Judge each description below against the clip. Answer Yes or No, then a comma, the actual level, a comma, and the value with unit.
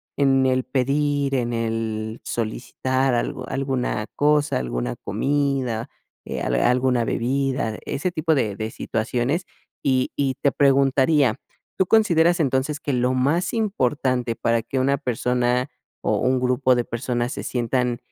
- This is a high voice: No, low, 130 Hz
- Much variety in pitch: No, average, 2.7 semitones